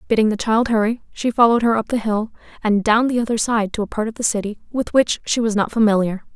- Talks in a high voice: Yes, high, 220 Hz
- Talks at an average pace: No, fast, 255 wpm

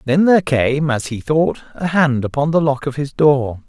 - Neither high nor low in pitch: Yes, medium, 145 Hz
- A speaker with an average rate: No, fast, 230 wpm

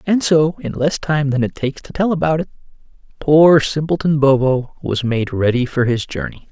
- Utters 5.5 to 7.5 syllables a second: No, 5.0 syllables/s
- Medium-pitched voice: Yes, medium, 145 Hz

